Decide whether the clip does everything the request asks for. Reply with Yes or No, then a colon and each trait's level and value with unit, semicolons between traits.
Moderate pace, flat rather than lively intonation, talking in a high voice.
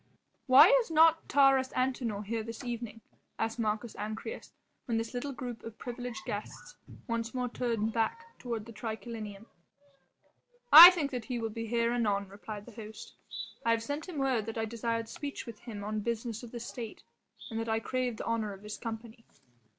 Yes: average, 185 wpm; narrow, 2.2 semitones; high, 230 Hz